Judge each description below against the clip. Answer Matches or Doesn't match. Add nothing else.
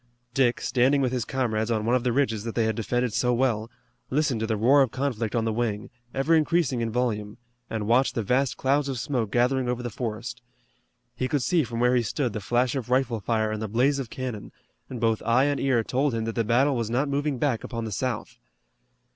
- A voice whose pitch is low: Matches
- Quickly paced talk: Matches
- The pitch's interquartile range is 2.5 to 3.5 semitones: Matches